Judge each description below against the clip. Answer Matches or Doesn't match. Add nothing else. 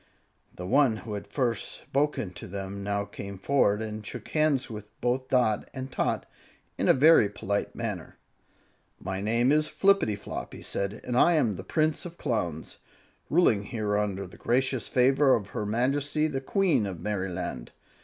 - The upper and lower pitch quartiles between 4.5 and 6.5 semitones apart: Matches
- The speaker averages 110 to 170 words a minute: Matches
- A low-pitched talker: Matches